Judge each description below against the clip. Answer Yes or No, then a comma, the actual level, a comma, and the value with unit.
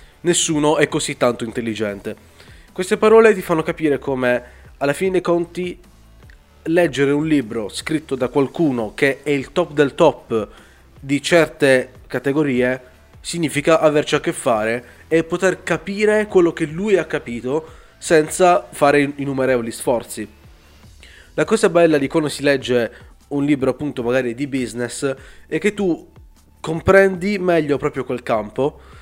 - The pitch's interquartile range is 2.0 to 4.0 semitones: No, wide, 5.5 semitones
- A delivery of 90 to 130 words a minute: No, average, 140 wpm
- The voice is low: No, medium, 145 Hz